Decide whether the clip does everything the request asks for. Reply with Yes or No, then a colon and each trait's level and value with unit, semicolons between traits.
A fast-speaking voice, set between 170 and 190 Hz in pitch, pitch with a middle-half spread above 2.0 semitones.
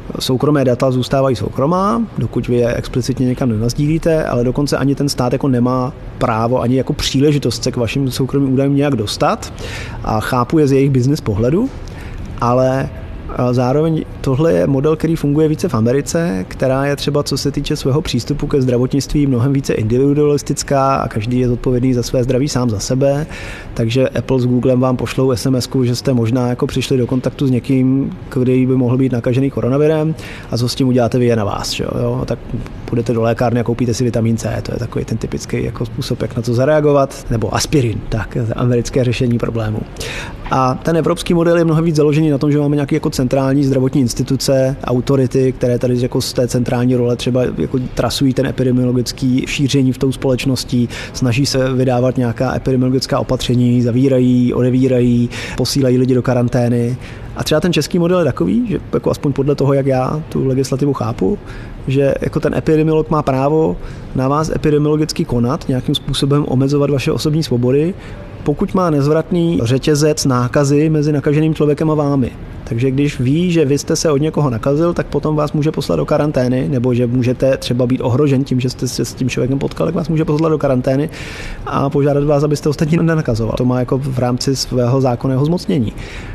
No: fast, 185 wpm; low, 130 Hz; average, 2.8 semitones